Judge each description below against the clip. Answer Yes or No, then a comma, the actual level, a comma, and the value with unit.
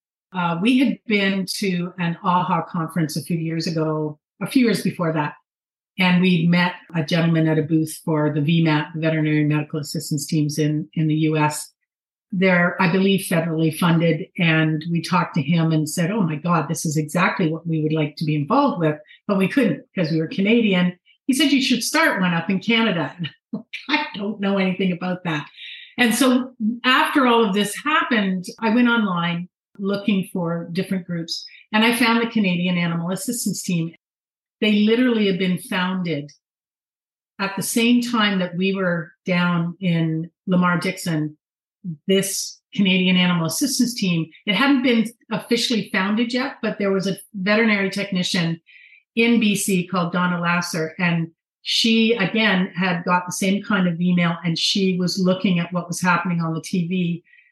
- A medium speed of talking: Yes, average, 175 wpm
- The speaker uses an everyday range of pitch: Yes, average, 4.2 semitones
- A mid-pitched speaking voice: Yes, medium, 180 Hz